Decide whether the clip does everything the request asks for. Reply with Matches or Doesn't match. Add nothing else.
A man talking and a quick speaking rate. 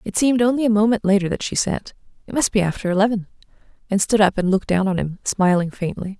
Doesn't match